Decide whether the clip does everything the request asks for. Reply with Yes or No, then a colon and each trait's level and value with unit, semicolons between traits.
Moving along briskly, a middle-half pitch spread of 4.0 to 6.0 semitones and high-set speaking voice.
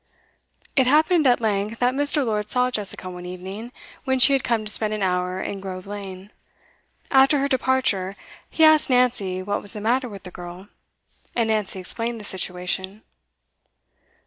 No: average, 170 wpm; average, 5.0 semitones; high, 215 Hz